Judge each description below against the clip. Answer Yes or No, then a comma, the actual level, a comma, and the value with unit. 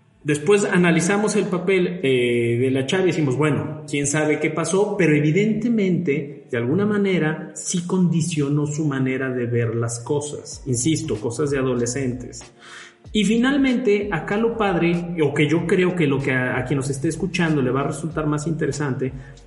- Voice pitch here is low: No, medium, 155 Hz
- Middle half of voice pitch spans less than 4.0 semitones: No, average, 4.8 semitones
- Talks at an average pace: Yes, average, 175 wpm